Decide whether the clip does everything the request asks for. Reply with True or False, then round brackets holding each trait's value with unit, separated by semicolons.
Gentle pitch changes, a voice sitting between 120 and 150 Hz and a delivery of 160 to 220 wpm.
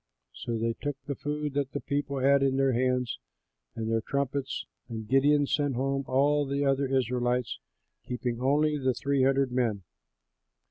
True (2.2 semitones; 135 Hz; 165 wpm)